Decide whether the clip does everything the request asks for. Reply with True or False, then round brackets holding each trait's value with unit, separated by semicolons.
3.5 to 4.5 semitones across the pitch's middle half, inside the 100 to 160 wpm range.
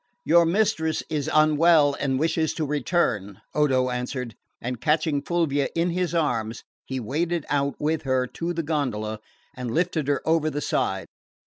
True (4.0 semitones; 155 wpm)